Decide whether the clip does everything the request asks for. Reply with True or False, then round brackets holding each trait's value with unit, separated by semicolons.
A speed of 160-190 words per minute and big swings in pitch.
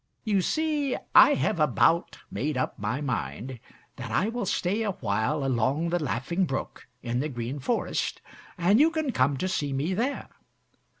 True (170 wpm; 8.3 semitones)